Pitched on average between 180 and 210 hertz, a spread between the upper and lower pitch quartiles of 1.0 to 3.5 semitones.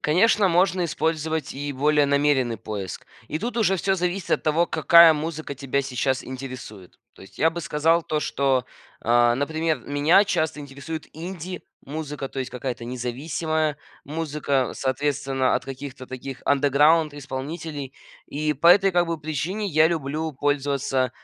No: medium, 150 Hz; average, 3.2 semitones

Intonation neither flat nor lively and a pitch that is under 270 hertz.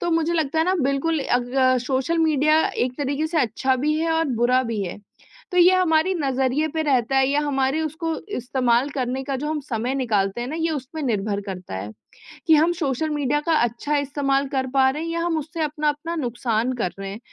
No: average, 4.0 semitones; very high, 275 Hz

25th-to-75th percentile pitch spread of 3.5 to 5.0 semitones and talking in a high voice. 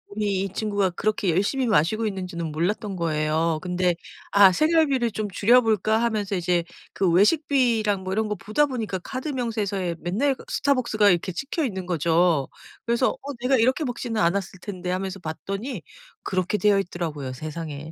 Yes: average, 4.5 semitones; high, 200 Hz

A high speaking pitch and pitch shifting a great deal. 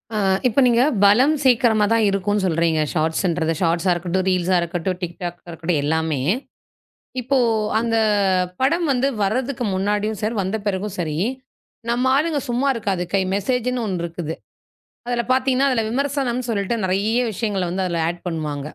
Yes: high, 200 Hz; wide, 5.9 semitones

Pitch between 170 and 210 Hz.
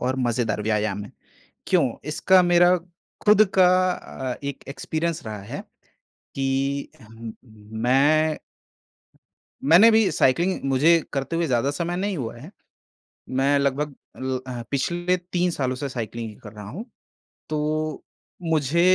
No: medium, 145 Hz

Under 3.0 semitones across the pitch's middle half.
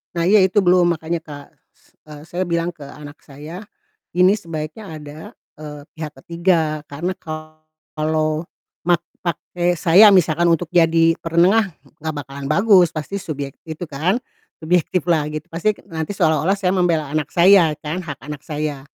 Yes: narrow, 2.6 semitones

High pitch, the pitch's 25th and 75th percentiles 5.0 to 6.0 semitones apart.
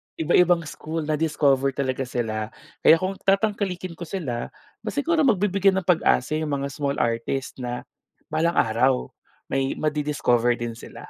No: medium, 150 Hz; wide, 5.5 semitones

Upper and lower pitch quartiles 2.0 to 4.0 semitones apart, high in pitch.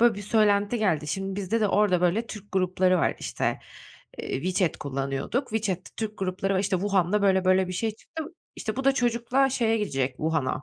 Yes: average, 3.3 semitones; high, 195 Hz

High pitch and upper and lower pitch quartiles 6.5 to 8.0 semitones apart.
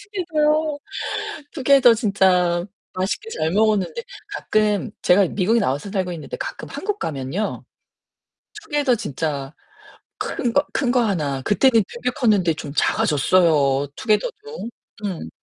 Yes: high, 210 Hz; wide, 7.4 semitones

